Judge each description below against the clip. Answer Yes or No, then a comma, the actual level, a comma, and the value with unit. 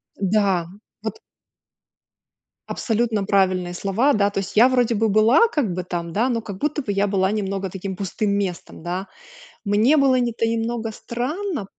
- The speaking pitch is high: Yes, high, 210 Hz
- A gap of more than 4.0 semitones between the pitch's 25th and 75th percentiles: No, average, 3.7 semitones